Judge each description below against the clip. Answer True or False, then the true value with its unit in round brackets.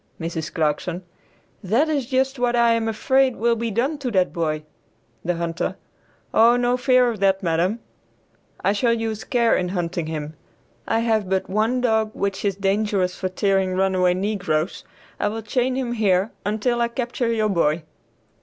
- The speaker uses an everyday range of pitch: True (4.5 semitones)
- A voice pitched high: True (210 Hz)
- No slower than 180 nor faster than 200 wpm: False (170 wpm)